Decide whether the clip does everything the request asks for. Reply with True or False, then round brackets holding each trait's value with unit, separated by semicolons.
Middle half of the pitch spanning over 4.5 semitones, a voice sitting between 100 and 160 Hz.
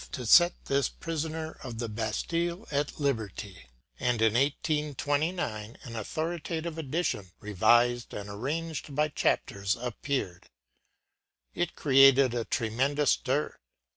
True (5.6 semitones; 135 Hz)